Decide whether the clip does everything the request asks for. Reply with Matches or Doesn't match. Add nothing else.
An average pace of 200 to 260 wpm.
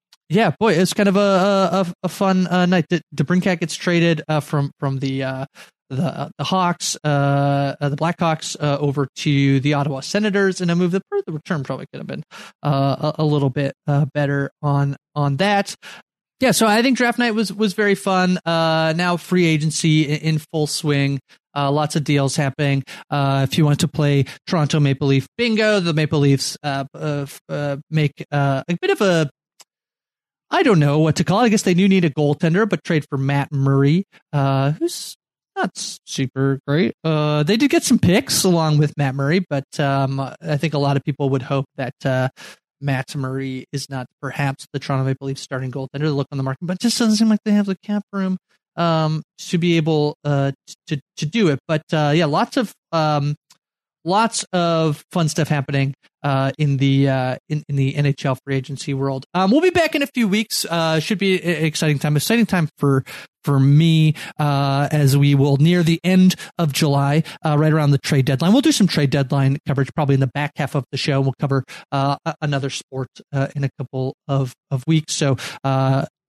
Matches